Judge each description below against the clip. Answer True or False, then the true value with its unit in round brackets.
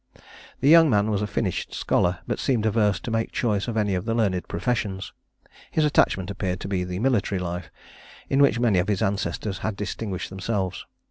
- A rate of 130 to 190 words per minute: False (200 wpm)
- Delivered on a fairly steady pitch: False (3.4 semitones)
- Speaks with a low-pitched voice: True (100 Hz)